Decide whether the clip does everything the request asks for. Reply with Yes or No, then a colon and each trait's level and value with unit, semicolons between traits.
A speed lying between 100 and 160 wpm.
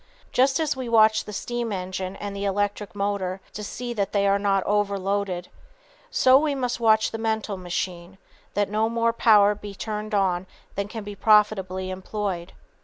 No: average, 175 wpm